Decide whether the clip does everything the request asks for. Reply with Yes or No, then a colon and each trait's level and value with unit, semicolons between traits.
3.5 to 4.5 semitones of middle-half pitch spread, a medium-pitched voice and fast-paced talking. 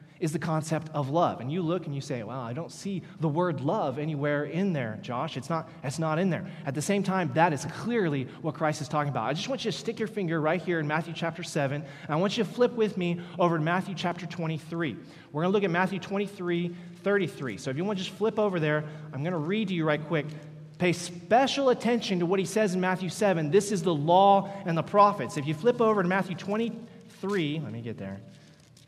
Yes: average, 4.1 semitones; medium, 175 Hz; fast, 250 wpm